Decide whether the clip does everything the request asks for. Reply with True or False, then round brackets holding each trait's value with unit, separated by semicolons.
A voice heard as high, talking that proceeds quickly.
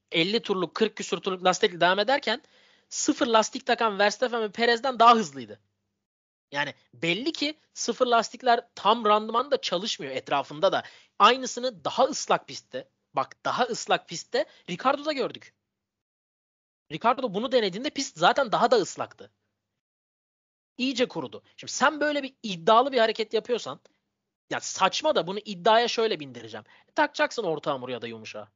True (225 Hz; 145 wpm)